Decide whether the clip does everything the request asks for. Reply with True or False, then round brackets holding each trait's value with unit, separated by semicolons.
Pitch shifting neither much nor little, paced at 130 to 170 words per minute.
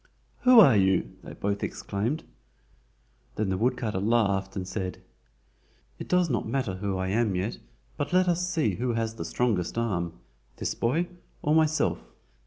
False (5.9 semitones; 155 wpm)